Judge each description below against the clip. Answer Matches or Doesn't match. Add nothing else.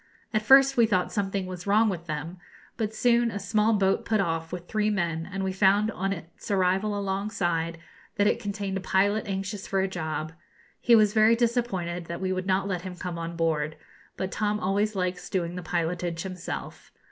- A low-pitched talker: Doesn't match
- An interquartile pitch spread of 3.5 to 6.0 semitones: Doesn't match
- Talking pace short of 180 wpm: Doesn't match